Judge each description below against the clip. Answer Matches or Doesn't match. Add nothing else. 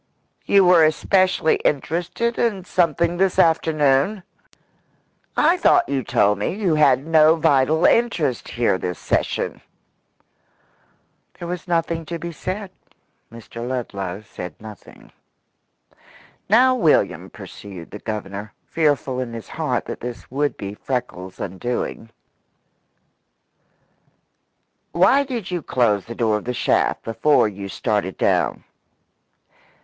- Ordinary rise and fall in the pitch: Doesn't match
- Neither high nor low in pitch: Matches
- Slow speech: Matches